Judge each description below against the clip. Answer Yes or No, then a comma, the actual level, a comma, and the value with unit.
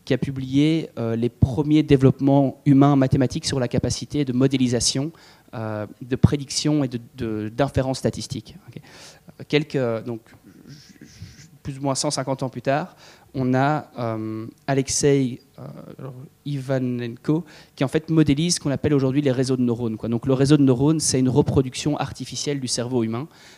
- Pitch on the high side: No, low, 135 Hz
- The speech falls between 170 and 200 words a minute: No, average, 160 wpm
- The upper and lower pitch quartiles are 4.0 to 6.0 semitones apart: No, average, 3.1 semitones